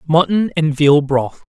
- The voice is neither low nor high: Yes, medium, 155 Hz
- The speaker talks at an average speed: Yes, average, 160 wpm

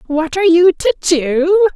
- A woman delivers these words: No, male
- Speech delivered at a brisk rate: No, average, 170 wpm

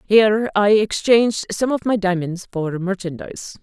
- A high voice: Yes, high, 200 Hz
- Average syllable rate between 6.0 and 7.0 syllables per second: No, 4.8 syllables/s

